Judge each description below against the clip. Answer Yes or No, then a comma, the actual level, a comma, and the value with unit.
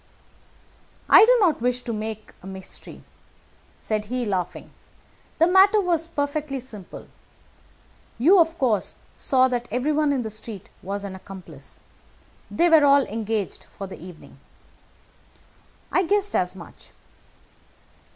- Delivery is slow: Yes, slow, 130 wpm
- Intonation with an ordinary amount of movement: No, wide, 7.5 semitones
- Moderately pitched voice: No, high, 245 Hz